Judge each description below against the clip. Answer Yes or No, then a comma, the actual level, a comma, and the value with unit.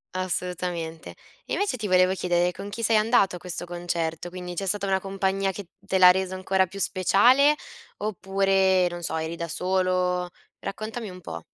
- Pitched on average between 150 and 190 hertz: Yes, medium, 185 Hz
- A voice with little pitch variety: Yes, narrow, 1.7 semitones